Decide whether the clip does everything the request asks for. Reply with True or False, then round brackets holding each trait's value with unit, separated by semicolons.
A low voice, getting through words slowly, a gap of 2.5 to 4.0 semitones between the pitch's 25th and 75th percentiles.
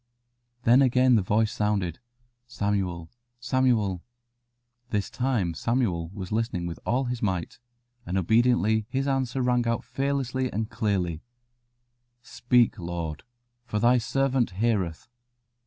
False (115 Hz; 120 wpm; 4.9 semitones)